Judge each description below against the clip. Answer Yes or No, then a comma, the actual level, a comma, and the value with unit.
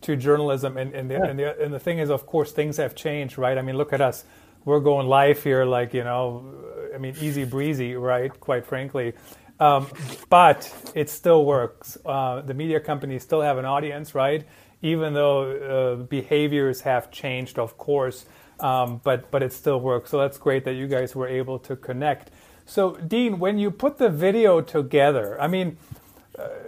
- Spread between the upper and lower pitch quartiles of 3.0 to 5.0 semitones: No, narrow, 2.6 semitones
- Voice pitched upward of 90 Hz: Yes, medium, 140 Hz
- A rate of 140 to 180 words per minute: No, average, 190 wpm